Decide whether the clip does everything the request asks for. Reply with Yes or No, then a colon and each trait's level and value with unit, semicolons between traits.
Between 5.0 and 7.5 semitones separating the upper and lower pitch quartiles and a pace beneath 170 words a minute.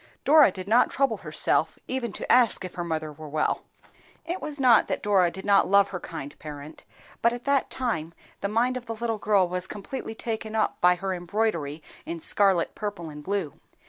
No: wide, 5.5 semitones; average, 200 wpm